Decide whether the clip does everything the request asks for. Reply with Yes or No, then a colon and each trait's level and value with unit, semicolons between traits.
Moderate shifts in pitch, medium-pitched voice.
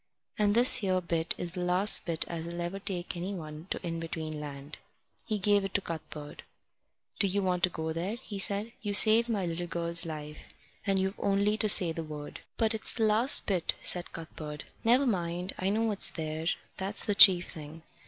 Yes: average, 3.7 semitones; medium, 180 Hz